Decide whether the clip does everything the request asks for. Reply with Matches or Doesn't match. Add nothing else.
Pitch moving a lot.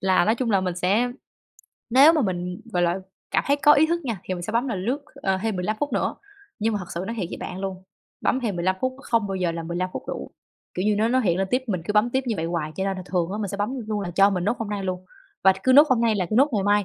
Doesn't match